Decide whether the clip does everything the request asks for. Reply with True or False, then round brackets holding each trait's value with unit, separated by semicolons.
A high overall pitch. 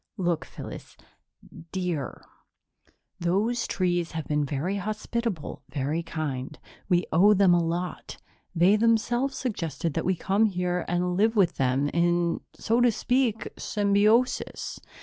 False (180 Hz)